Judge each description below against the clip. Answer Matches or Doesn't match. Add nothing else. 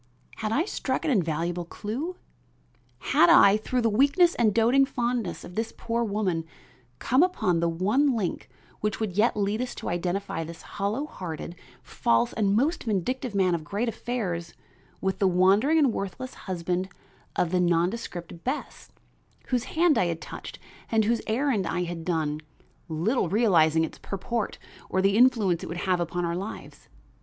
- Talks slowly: Doesn't match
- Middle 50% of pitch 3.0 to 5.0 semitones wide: Doesn't match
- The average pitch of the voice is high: Matches